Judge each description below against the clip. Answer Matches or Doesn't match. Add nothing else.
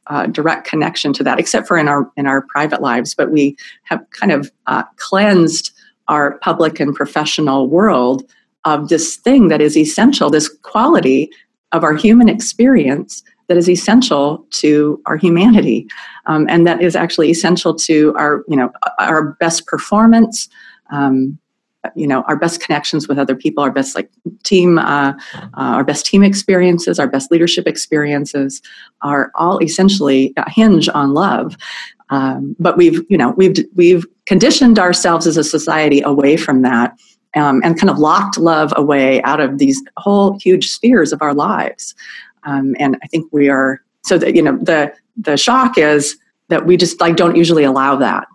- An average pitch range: Matches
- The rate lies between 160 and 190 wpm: Matches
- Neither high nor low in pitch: Matches